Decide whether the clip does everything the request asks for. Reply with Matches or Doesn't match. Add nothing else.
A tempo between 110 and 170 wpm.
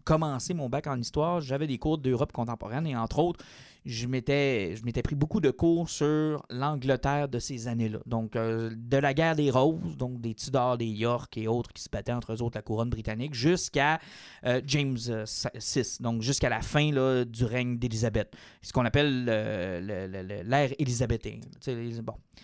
Doesn't match